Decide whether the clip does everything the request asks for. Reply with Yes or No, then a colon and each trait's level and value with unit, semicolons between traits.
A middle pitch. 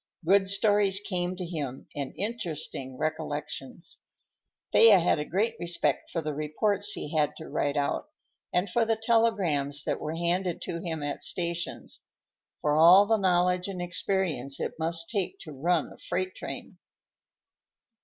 Yes: medium, 175 Hz